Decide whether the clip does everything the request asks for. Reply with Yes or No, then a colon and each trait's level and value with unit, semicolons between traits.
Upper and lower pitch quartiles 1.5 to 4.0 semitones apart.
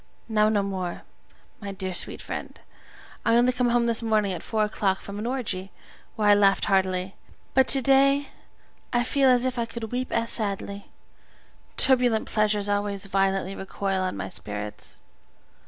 Yes: average, 3.7 semitones